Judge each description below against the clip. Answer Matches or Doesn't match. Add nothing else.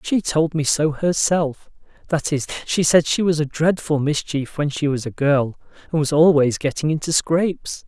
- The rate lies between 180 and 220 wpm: Matches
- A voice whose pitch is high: Doesn't match